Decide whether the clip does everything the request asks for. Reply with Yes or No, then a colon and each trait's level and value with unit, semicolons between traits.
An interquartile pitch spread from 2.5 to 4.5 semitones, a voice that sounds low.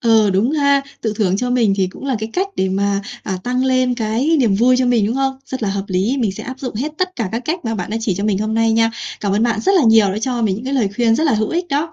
No: average, 3.9 semitones; high, 230 Hz